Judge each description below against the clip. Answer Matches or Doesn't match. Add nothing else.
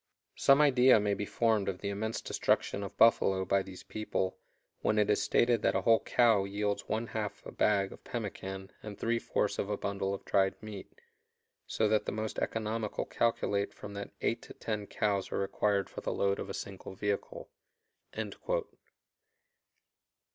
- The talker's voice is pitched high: Doesn't match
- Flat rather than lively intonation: Matches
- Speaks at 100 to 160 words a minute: Doesn't match